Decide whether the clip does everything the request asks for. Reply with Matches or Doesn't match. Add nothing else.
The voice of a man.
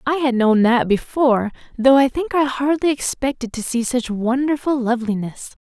Doesn't match